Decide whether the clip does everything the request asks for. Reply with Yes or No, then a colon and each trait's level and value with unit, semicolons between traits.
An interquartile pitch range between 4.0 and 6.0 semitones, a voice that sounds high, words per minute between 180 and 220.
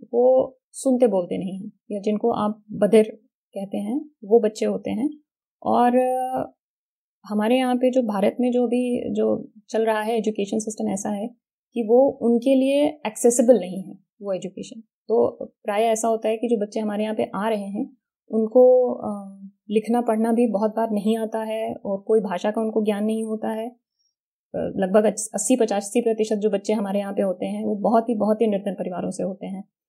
No: narrow, 2.5 semitones; high, 220 Hz; average, 185 wpm